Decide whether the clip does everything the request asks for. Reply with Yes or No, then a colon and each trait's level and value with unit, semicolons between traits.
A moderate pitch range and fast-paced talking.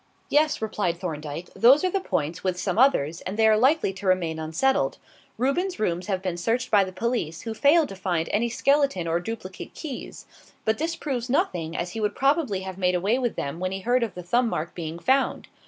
No: wide, 6.3 semitones; fast, 215 wpm